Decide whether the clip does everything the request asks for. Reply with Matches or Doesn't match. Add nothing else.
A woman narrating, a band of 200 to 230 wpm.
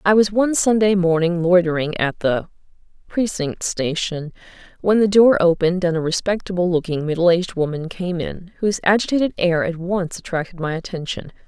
Doesn't match